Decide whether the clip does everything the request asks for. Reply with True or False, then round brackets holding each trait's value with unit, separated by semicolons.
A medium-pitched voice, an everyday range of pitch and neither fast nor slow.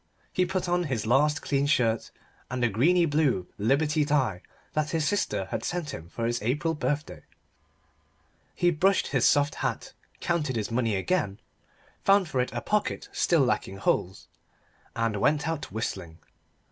False (145 Hz; 6.1 semitones; 160 wpm)